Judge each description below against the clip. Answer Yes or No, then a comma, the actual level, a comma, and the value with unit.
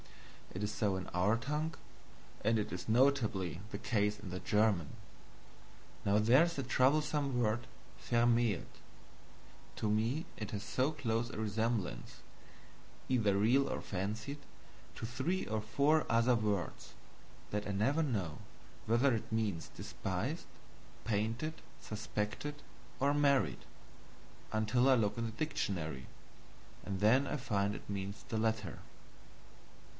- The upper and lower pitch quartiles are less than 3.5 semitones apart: No, average, 4.2 semitones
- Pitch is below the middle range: Yes, low, 110 Hz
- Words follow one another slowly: Yes, slow, 130 wpm